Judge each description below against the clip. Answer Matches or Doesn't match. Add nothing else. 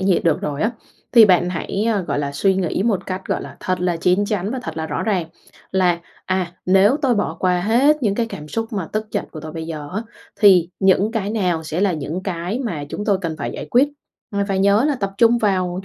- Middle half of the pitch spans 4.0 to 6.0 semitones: Doesn't match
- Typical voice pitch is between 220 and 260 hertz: Doesn't match